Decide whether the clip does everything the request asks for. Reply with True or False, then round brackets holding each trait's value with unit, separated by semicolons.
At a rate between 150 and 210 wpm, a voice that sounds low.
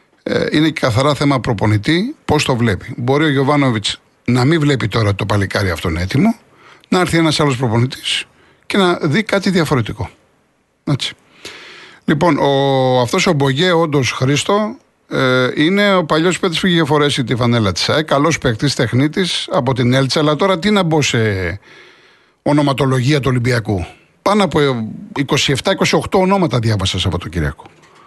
False (155 wpm; 145 Hz)